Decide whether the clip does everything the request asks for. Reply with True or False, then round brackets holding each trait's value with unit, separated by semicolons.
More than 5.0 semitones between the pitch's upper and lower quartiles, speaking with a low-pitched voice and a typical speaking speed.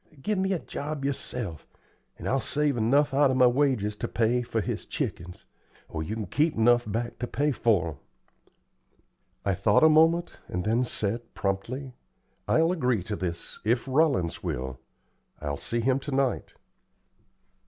True (5.4 semitones; 120 Hz; 165 wpm)